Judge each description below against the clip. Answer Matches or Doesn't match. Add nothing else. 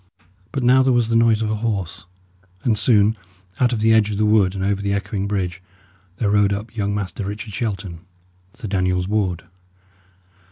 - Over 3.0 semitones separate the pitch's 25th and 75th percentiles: Doesn't match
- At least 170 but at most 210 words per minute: Matches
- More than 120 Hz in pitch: Doesn't match